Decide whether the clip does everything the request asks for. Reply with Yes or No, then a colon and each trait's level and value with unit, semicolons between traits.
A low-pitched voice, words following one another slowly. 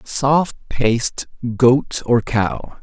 Yes: low, 125 Hz; slow, 105 wpm